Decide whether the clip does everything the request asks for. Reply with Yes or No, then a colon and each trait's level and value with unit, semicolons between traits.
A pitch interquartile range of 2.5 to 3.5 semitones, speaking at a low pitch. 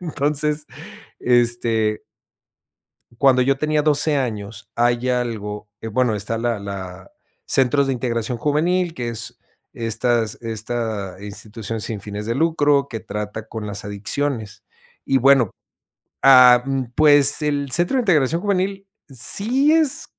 No: average, 4.9 semitones; low, 125 Hz